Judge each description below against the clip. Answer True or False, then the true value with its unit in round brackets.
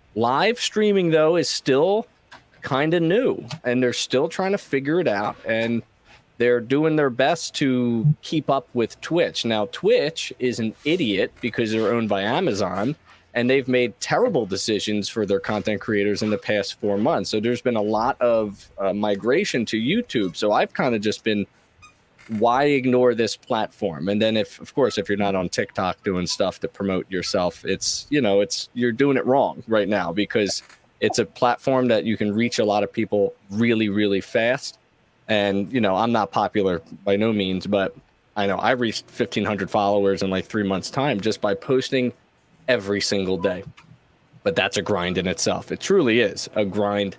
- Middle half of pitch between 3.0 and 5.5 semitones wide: True (3.7 semitones)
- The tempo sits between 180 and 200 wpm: True (190 wpm)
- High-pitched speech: False (110 Hz)